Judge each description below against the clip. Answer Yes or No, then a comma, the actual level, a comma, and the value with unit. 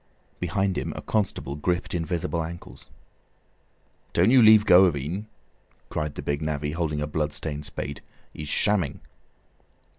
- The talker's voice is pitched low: Yes, very low, 85 Hz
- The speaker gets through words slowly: No, average, 145 wpm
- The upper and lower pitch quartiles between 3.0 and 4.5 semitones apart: Yes, average, 3.9 semitones